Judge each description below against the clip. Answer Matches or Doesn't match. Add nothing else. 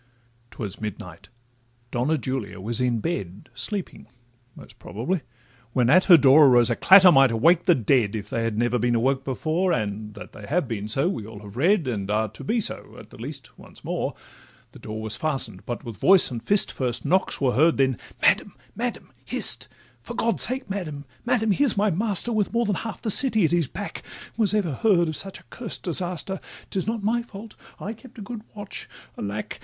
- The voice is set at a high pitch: Doesn't match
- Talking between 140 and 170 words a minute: Doesn't match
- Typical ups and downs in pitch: Doesn't match